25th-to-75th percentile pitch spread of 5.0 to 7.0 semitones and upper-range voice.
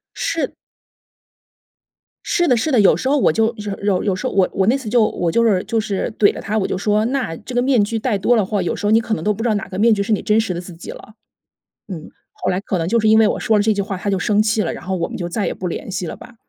No: average, 2.8 semitones; high, 210 Hz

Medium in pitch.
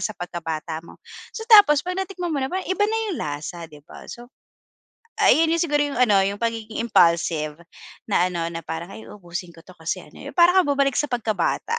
No: high, 220 Hz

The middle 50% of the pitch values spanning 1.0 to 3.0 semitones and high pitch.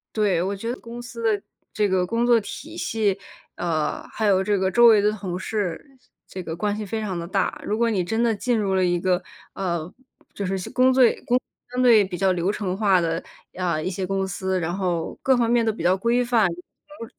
No: average, 3.9 semitones; high, 200 Hz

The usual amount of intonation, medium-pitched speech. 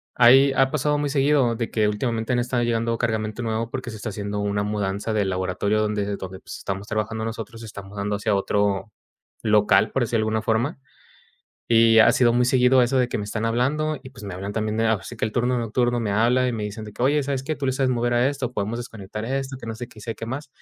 No: average, 3.1 semitones; low, 115 Hz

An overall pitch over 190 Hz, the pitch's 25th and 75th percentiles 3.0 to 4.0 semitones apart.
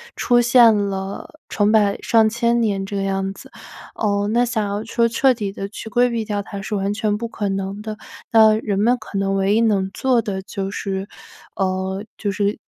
No: high, 205 Hz; narrow, 2.4 semitones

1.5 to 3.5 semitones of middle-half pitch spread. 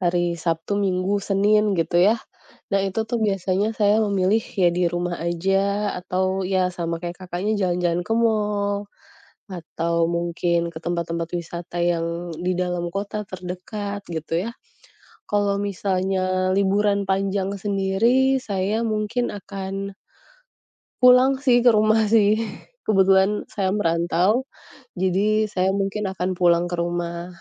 Yes: average, 2.9 semitones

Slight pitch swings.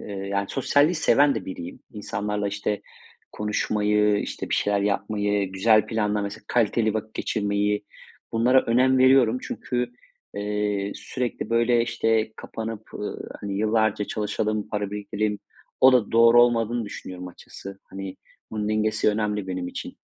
Yes: narrow, 2.0 semitones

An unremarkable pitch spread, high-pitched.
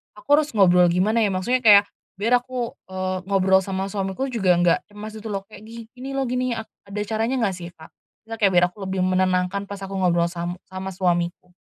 Yes: average, 3.2 semitones; high, 195 Hz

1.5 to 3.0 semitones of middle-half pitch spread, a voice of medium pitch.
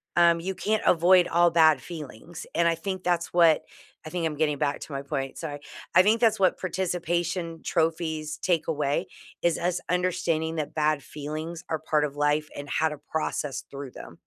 Yes: narrow, 2.5 semitones; medium, 165 Hz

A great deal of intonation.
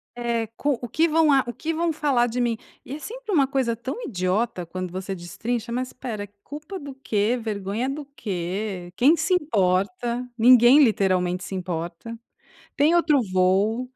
Yes: wide, 6.5 semitones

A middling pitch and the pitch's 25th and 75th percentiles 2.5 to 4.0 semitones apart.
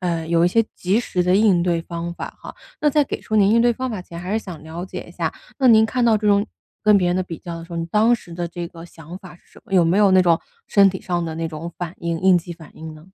Yes: medium, 180 Hz; average, 3.6 semitones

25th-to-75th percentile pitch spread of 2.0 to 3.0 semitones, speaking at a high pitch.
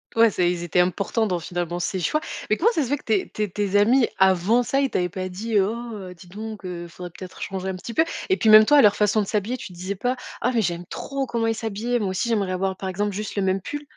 No: average, 3.7 semitones; high, 205 Hz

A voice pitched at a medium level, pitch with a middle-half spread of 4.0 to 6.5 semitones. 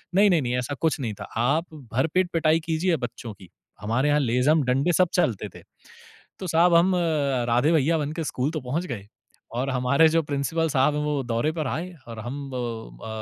Yes: medium, 145 Hz; average, 4.5 semitones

